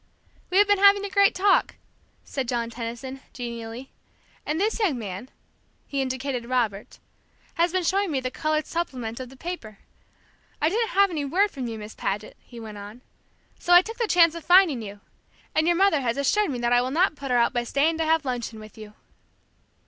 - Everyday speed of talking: No, fast, 210 wpm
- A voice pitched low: No, very high, 270 Hz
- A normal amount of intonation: No, wide, 6.9 semitones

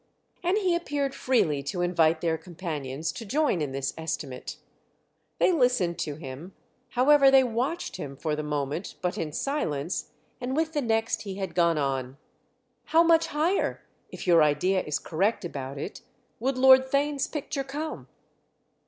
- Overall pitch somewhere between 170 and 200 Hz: Yes, high, 190 Hz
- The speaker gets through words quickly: No, average, 155 wpm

